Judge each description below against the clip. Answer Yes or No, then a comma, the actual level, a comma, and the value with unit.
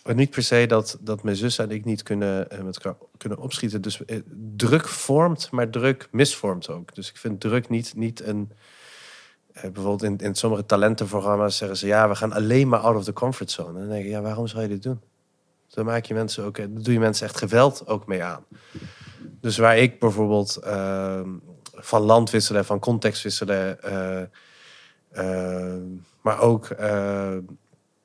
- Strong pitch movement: No, narrow, 2.5 semitones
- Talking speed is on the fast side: No, average, 180 wpm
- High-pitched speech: No, low, 105 Hz